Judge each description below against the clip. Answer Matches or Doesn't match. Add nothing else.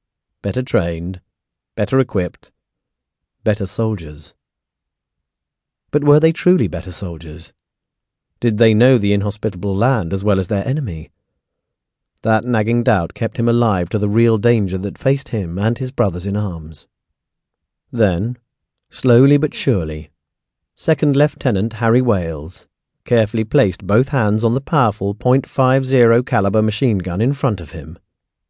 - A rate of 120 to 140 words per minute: Matches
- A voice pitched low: Matches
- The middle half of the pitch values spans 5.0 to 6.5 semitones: Matches